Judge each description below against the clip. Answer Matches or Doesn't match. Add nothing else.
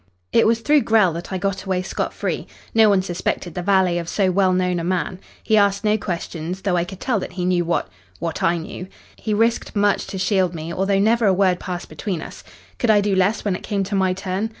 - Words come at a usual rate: Doesn't match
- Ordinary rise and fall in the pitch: Doesn't match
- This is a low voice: Doesn't match